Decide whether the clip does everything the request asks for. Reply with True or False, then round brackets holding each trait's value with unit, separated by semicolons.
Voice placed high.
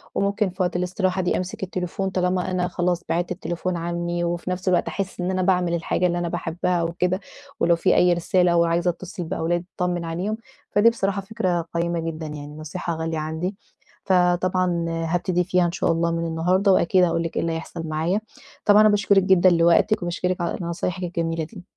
False (175 Hz)